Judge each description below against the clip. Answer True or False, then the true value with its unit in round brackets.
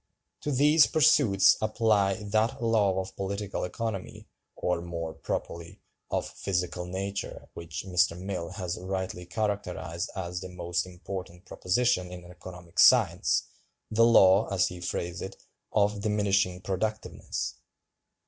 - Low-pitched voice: True (95 Hz)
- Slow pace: True (120 wpm)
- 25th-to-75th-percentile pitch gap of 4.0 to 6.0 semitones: False (2.8 semitones)